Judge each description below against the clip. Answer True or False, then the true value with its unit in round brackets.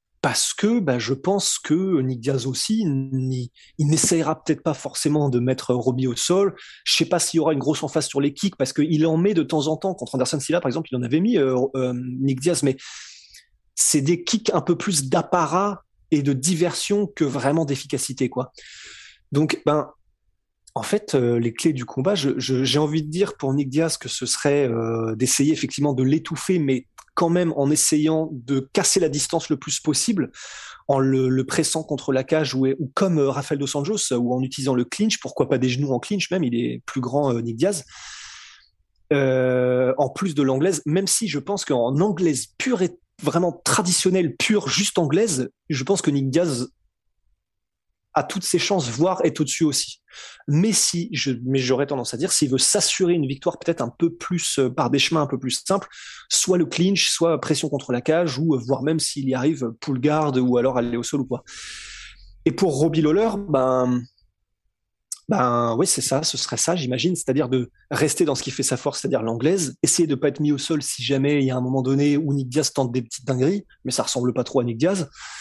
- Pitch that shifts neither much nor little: True (4.3 semitones)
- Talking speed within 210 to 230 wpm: True (220 wpm)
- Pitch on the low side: False (145 Hz)